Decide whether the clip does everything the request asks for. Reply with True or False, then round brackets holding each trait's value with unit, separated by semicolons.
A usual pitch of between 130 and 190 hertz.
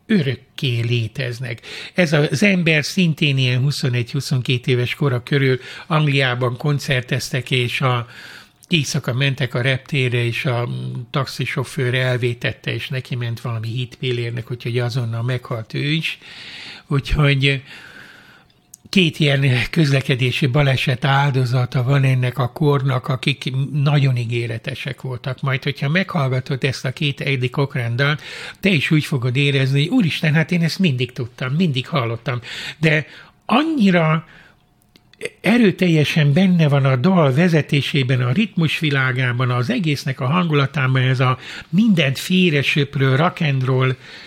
True (140 Hz)